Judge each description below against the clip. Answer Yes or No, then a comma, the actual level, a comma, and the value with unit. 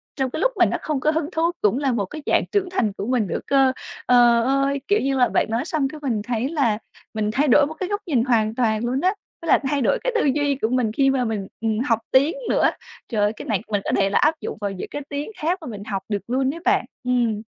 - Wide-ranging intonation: No, average, 4.9 semitones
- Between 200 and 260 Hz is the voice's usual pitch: Yes, very high, 255 Hz